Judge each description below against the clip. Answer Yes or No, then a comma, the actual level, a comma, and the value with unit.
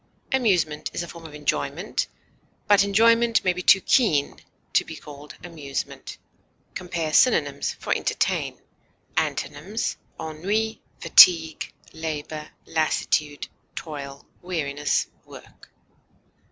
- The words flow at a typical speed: No, slow, 100 wpm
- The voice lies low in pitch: No, medium, 160 Hz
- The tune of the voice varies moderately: Yes, average, 4.7 semitones